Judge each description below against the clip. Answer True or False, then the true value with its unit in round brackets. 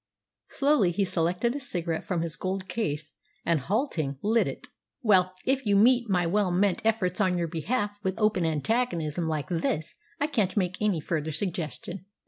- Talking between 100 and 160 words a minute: False (170 wpm)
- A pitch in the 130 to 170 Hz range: False (185 Hz)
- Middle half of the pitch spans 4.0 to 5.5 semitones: True (4.3 semitones)